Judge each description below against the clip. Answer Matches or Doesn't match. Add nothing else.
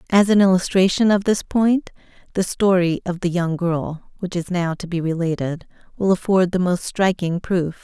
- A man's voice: Doesn't match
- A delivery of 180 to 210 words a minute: Matches